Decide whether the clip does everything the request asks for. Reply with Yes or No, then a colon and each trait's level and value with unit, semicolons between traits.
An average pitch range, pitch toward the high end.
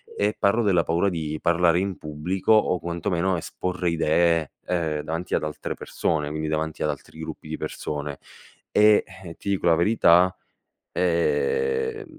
No: average, 3.5 semitones; very low, 85 Hz